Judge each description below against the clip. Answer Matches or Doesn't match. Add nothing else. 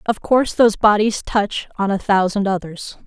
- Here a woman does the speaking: Matches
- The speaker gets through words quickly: Doesn't match